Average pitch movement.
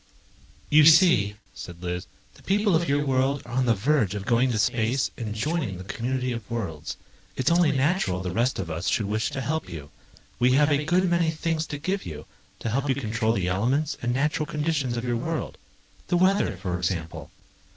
No: wide, 6.7 semitones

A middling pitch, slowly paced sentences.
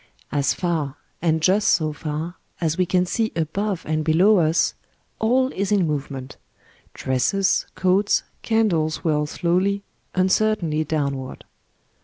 Yes: medium, 170 Hz; slow, 130 wpm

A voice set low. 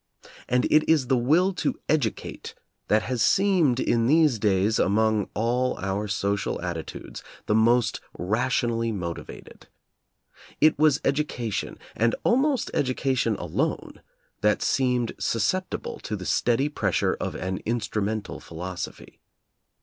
Yes: low, 115 Hz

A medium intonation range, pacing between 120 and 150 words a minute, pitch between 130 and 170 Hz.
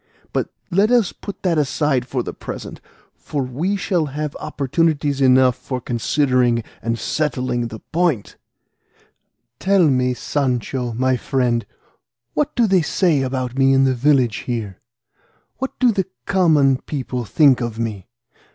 Yes: average, 4.2 semitones; average, 140 wpm; low, 135 Hz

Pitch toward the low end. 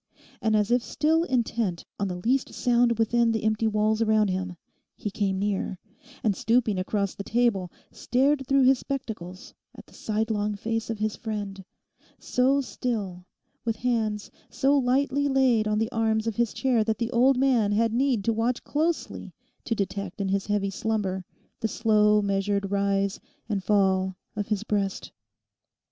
No: high, 220 Hz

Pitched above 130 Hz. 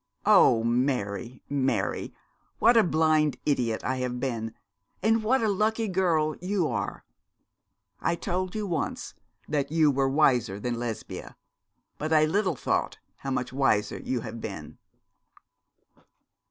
Yes: medium, 140 Hz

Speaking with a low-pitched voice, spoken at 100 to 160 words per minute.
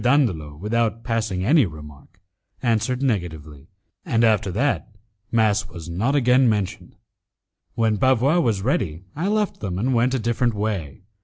Yes: low, 110 Hz; average, 145 wpm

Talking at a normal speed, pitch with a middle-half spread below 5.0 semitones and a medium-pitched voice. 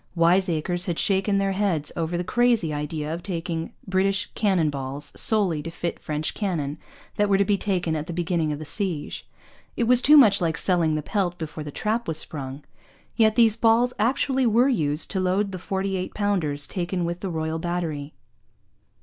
Yes: average, 190 wpm; average, 4.3 semitones; medium, 180 Hz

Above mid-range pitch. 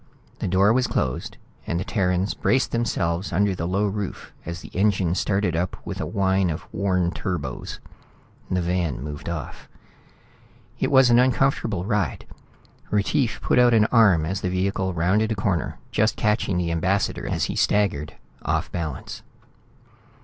No: very low, 95 Hz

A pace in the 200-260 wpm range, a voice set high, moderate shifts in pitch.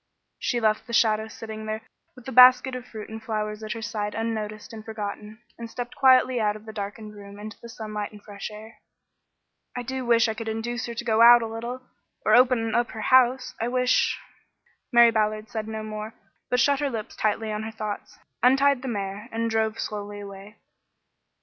No: fast, 205 wpm; high, 220 Hz; narrow, 2.1 semitones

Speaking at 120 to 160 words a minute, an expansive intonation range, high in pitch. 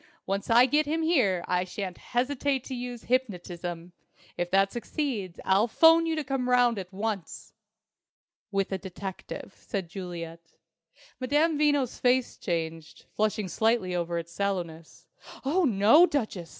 Yes: average, 140 wpm; wide, 6.3 semitones; high, 210 Hz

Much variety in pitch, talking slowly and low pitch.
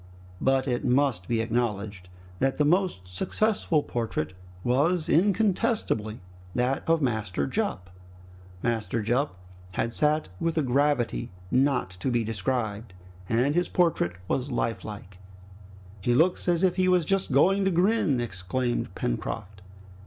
Yes: wide, 7.1 semitones; slow, 130 wpm; low, 125 Hz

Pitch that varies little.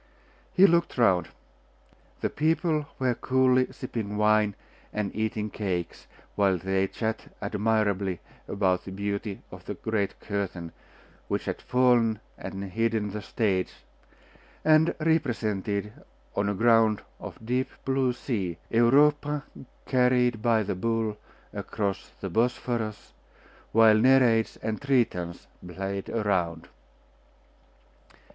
No: average, 4.0 semitones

